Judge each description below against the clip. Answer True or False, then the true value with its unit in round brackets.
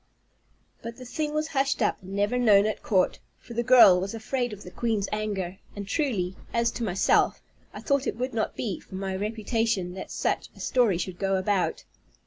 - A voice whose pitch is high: True (215 Hz)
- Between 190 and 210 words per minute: True (200 wpm)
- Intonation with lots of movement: False (3.9 semitones)